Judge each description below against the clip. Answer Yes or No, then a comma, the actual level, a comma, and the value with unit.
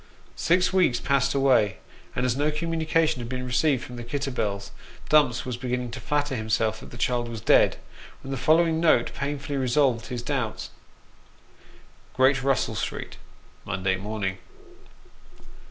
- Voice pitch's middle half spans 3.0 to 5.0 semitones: Yes, average, 3.5 semitones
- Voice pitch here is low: Yes, low, 130 Hz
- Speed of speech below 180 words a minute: Yes, average, 145 wpm